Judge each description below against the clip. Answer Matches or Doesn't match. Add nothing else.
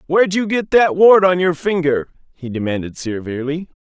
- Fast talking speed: Doesn't match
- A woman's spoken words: Doesn't match